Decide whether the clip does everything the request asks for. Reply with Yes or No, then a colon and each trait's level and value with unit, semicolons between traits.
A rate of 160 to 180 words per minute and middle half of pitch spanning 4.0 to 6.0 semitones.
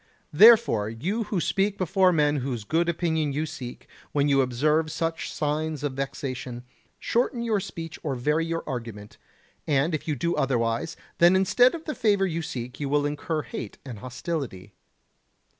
Yes: average, 165 wpm; average, 4.7 semitones